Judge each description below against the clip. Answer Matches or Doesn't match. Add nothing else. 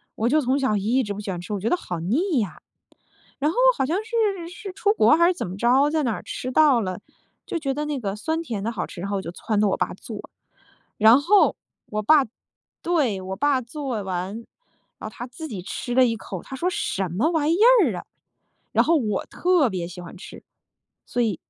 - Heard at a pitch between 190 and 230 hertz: Doesn't match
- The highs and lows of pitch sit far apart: Matches